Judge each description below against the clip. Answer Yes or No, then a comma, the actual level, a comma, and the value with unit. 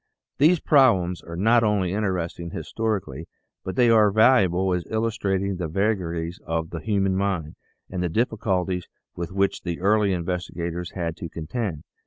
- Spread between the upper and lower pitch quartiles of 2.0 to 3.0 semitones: No, average, 3.8 semitones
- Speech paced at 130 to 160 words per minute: Yes, average, 155 wpm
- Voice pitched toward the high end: No, very low, 95 Hz